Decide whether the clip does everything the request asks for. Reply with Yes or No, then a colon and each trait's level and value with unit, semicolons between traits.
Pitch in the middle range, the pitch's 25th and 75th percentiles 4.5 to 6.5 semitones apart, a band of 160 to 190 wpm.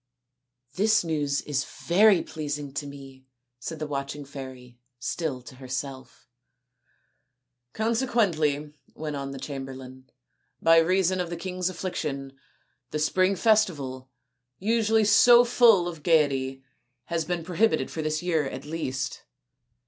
No: medium, 150 Hz; average, 5.2 semitones; slow, 135 wpm